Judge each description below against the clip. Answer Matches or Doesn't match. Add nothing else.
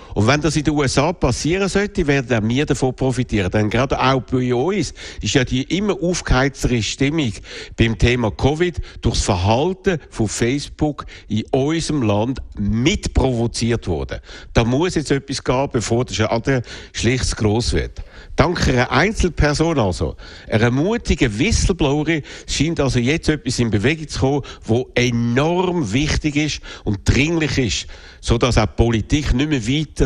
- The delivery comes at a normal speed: Matches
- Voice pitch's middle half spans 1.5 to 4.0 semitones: Doesn't match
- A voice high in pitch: Doesn't match